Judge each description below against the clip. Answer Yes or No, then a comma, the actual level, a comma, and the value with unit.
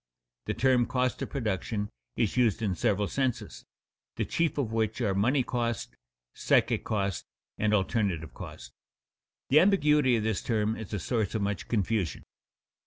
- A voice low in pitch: Yes, low, 110 Hz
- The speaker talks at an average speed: Yes, average, 155 wpm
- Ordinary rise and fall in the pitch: Yes, average, 3.8 semitones